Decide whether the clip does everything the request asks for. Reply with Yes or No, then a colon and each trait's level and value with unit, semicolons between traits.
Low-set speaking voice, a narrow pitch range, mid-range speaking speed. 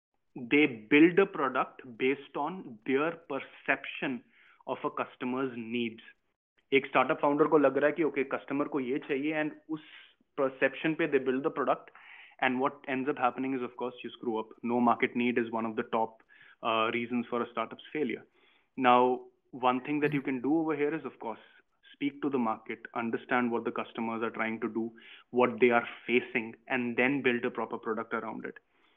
No: low, 125 Hz; average, 3.5 semitones; average, 190 wpm